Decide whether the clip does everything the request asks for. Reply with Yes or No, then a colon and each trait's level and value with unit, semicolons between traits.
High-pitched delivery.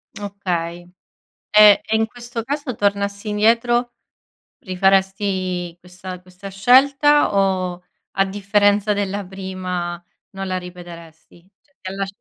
Yes: high, 195 Hz